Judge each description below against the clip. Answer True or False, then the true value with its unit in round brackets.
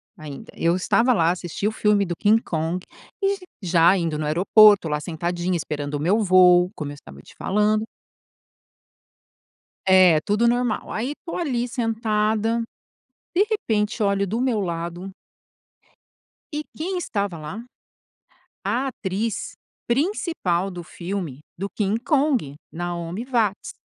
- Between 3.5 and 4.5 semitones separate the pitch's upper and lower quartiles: False (5.0 semitones)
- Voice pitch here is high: True (200 Hz)